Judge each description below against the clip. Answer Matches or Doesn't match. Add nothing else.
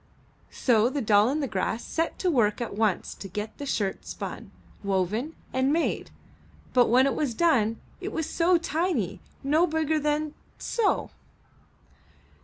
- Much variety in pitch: Matches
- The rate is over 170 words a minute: Doesn't match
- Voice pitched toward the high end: Matches